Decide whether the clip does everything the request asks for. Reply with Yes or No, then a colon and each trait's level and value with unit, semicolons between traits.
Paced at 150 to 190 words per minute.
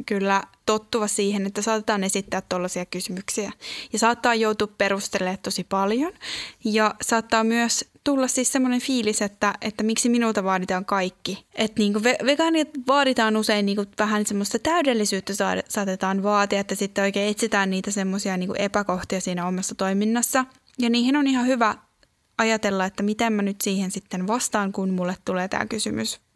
Yes: fast, 155 wpm